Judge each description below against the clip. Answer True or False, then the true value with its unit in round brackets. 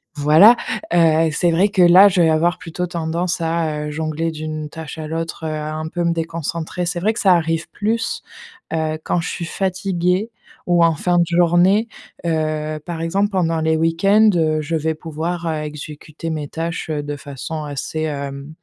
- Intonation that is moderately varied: False (2.0 semitones)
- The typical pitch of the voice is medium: True (165 Hz)